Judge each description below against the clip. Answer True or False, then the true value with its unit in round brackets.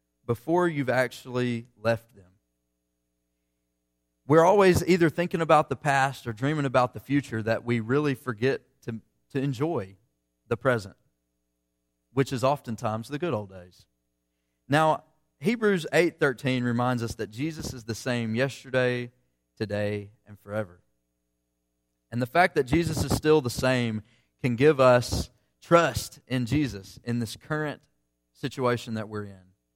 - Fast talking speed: False (140 wpm)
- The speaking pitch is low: True (120 Hz)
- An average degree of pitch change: False (7.2 semitones)